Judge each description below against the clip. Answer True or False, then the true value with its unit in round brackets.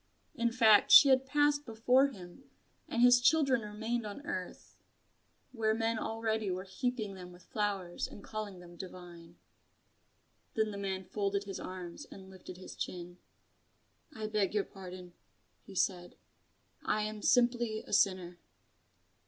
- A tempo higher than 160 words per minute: False (145 wpm)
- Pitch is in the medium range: False (210 Hz)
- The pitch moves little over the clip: False (3.8 semitones)